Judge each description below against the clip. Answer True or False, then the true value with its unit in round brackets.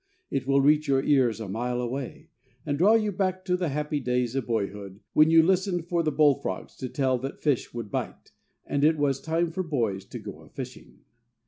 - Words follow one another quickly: True (210 wpm)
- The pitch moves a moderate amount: True (4.8 semitones)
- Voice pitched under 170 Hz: True (140 Hz)